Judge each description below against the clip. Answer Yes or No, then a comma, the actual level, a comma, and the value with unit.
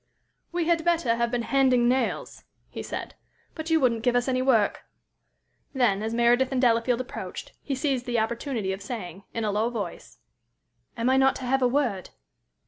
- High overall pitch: Yes, high, 245 Hz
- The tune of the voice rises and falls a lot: No, narrow, 2.6 semitones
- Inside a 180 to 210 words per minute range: Yes, average, 185 wpm